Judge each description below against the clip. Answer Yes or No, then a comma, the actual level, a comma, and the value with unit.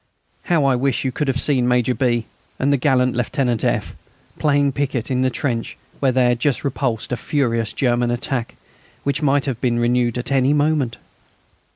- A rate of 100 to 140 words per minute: No, average, 185 wpm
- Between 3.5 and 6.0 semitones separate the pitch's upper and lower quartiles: No, narrow, 2.4 semitones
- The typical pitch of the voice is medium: No, low, 130 Hz